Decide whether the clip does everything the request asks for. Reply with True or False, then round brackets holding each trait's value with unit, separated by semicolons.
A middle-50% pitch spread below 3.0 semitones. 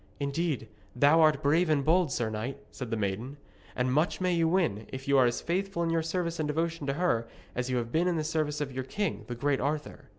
False (4.5 semitones)